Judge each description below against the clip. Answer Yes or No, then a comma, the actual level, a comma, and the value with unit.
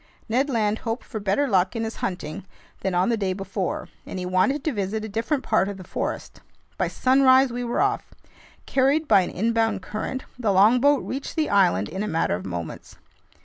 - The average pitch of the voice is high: Yes, high, 220 Hz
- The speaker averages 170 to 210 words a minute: Yes, average, 200 wpm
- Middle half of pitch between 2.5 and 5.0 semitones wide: No, wide, 5.4 semitones